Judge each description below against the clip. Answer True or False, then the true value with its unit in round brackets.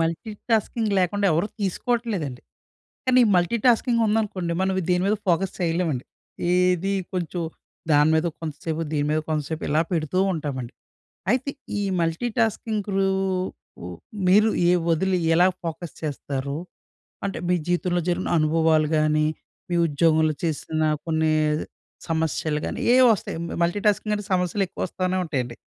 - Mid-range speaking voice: True (175 Hz)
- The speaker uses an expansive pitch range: False (4.0 semitones)